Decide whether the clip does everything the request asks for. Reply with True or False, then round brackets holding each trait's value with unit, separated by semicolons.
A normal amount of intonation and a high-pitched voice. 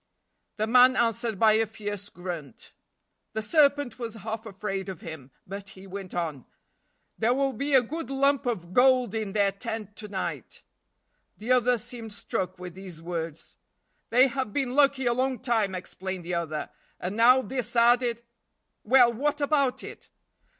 True (4.8 semitones; 225 Hz)